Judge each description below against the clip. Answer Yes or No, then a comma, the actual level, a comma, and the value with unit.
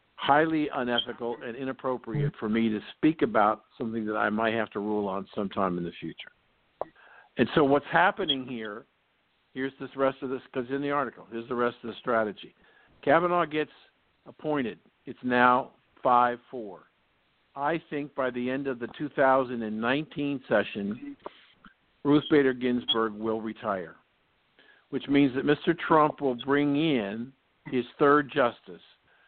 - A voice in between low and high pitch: No, low, 130 Hz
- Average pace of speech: Yes, average, 150 wpm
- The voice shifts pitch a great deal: No, average, 3.8 semitones